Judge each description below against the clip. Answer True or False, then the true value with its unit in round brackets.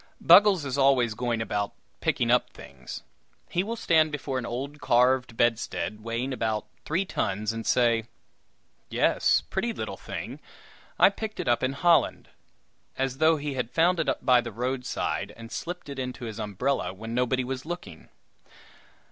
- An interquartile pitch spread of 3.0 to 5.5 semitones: True (4.6 semitones)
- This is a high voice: False (125 Hz)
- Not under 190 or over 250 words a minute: False (160 wpm)